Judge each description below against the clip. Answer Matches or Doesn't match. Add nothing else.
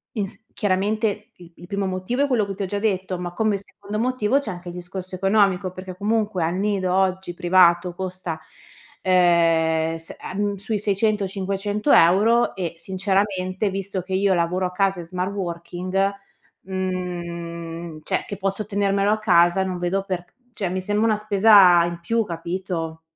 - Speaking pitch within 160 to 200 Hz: Matches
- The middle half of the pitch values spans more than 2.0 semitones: Matches